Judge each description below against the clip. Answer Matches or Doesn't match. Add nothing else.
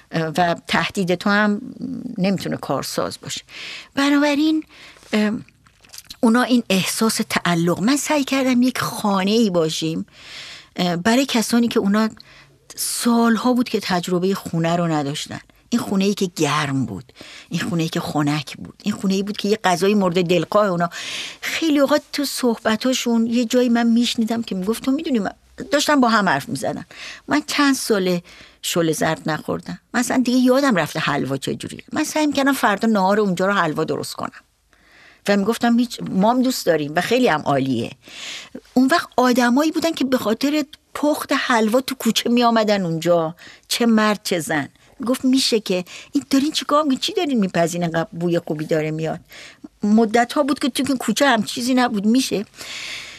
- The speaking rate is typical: Doesn't match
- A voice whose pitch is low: Doesn't match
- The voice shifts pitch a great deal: Matches